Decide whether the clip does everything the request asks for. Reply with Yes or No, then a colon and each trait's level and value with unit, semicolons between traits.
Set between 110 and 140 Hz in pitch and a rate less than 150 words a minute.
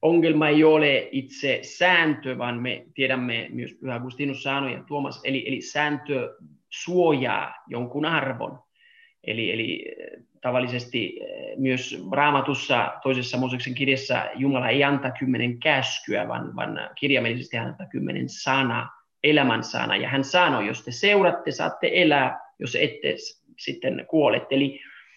Yes: low, 135 Hz; average, 125 wpm